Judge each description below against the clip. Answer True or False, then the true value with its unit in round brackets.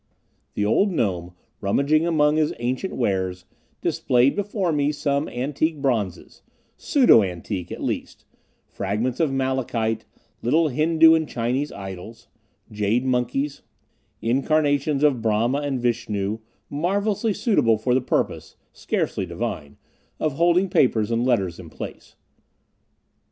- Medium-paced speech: False (120 wpm)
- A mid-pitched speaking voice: False (130 Hz)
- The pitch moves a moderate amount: False (5.7 semitones)